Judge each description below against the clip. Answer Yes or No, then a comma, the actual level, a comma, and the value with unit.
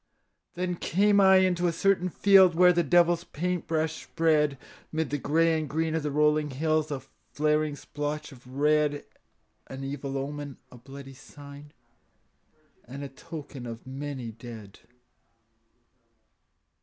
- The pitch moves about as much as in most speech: Yes, average, 3.1 semitones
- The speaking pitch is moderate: Yes, medium, 150 Hz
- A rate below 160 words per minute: Yes, average, 140 wpm